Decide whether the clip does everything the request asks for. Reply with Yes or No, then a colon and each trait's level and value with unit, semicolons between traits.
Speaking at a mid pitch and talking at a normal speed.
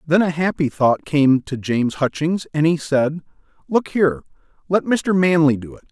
Yes: medium, 155 Hz; average, 185 wpm